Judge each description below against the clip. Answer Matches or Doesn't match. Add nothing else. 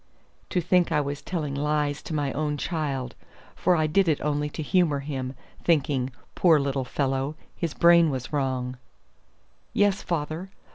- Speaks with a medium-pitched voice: Matches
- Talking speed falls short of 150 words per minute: Doesn't match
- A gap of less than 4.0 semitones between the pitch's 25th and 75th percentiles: Matches